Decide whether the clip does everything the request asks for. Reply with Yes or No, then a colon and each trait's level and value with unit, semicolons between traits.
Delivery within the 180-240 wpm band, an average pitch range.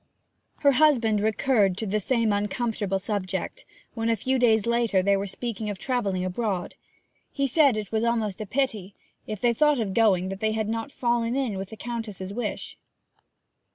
Yes: average, 185 wpm; average, 3.2 semitones